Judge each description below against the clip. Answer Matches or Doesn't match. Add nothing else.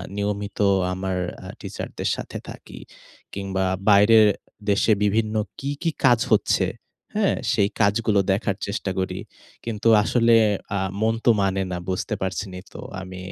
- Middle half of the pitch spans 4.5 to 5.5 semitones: Doesn't match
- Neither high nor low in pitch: Doesn't match